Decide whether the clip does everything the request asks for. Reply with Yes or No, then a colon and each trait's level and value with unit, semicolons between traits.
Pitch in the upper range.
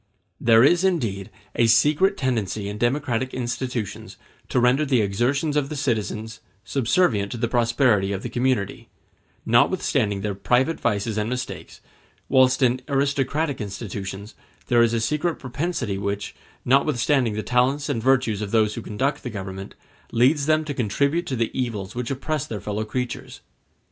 No: low, 120 Hz